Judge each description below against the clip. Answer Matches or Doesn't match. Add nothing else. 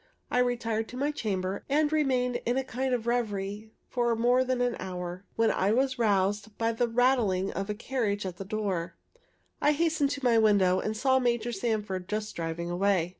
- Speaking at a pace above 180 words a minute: Matches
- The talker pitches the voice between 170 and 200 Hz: Doesn't match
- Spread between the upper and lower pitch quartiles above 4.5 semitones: Doesn't match